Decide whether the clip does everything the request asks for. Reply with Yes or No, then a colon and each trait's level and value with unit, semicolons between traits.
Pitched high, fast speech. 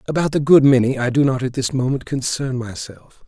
No: low, 135 Hz; fast, 220 wpm